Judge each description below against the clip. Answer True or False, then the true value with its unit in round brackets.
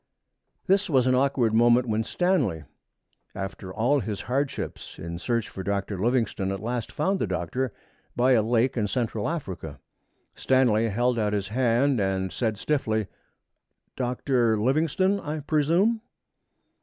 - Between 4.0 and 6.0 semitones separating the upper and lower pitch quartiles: True (4.5 semitones)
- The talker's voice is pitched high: False (120 Hz)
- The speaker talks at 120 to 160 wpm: True (145 wpm)